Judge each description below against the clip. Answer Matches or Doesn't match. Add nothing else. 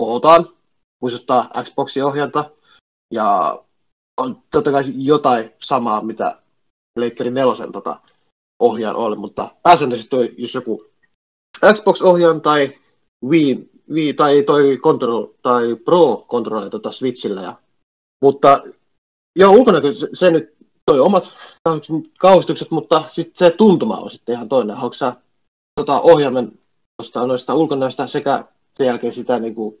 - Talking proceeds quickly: Doesn't match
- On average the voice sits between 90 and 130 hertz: Doesn't match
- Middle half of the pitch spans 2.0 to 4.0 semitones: Doesn't match